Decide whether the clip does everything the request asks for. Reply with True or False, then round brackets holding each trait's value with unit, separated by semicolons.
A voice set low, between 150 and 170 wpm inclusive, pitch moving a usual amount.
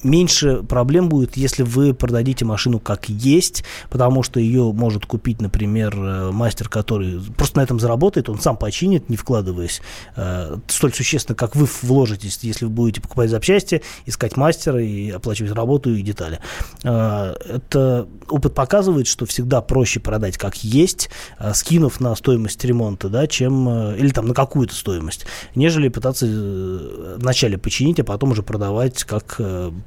True (120 Hz; 155 wpm; 3.9 semitones)